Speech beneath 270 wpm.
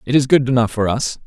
No: fast, 285 wpm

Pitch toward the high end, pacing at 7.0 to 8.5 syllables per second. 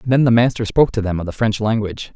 No: low, 110 Hz; 7.4 syllables/s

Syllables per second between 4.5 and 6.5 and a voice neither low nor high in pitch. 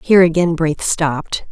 Yes: 5.0 syllables/s; medium, 165 Hz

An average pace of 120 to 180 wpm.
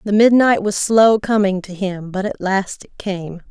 No: fast, 205 wpm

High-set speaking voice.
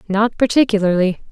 Yes: high, 205 Hz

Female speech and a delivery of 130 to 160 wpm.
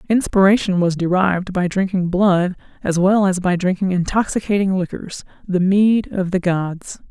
Yes: female; average, 145 wpm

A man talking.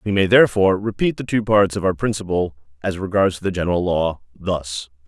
Yes: male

